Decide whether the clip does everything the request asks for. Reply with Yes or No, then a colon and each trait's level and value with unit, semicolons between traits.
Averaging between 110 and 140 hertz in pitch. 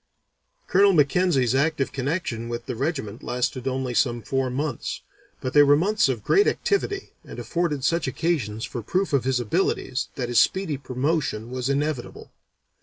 Yes: low, 135 Hz